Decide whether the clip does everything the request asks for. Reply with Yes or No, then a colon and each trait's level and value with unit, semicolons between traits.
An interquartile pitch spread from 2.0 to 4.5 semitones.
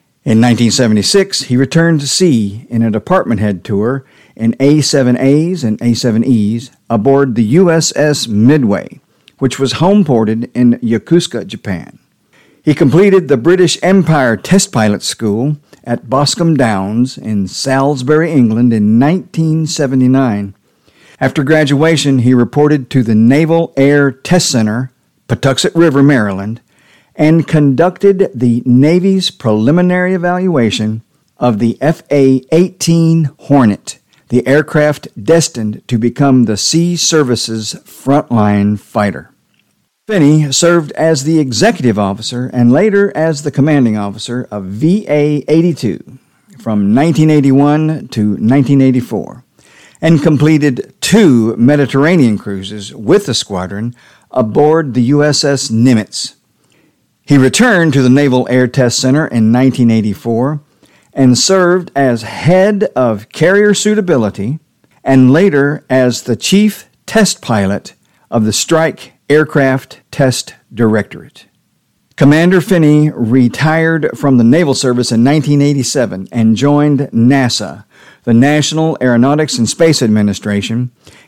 No: average, 5.1 semitones